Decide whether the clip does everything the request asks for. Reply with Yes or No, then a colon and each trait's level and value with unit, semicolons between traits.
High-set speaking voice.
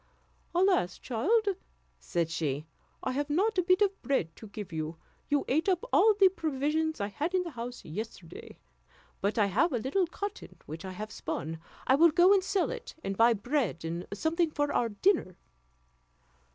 Yes: very high, 275 Hz